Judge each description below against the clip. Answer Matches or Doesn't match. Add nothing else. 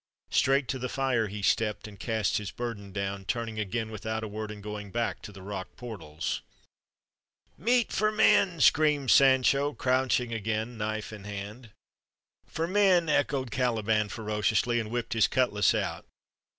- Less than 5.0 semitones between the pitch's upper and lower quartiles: Matches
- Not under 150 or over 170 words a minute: Matches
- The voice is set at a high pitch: Doesn't match